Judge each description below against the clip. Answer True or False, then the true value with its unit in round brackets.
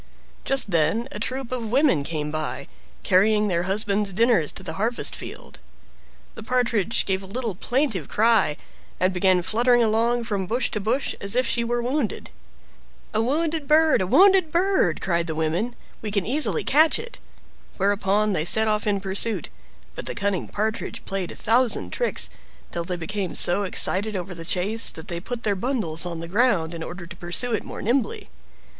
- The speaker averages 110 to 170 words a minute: False (180 wpm)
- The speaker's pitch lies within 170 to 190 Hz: False (210 Hz)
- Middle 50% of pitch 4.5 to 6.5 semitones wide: True (4.9 semitones)